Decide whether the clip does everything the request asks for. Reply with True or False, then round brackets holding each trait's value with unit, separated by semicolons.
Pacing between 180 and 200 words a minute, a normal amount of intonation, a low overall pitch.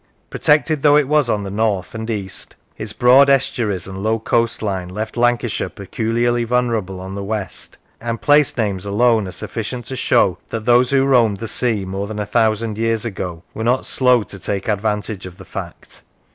True (185 wpm; 3.4 semitones; 110 Hz)